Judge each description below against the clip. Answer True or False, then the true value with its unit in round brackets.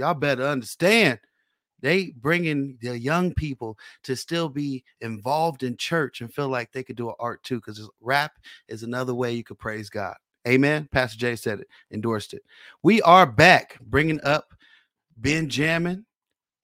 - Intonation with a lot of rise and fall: False (4.1 semitones)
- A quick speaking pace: False (160 wpm)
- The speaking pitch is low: True (130 Hz)